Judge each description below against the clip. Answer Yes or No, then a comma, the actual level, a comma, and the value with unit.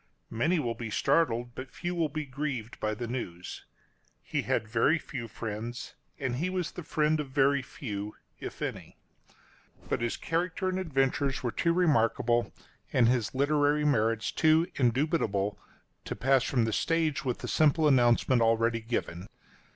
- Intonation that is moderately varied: Yes, average, 4.9 semitones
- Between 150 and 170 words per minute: Yes, average, 160 wpm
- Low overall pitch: Yes, low, 130 Hz